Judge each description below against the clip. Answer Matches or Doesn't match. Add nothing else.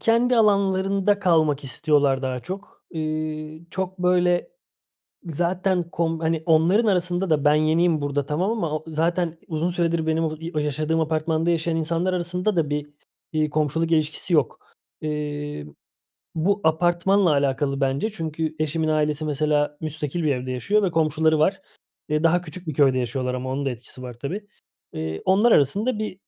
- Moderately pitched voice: Matches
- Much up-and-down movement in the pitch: Doesn't match